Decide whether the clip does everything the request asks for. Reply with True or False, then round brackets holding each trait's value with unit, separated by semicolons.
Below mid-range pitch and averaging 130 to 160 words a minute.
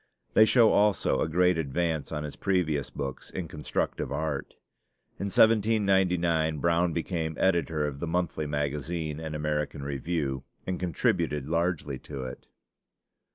True (80 Hz; 135 wpm)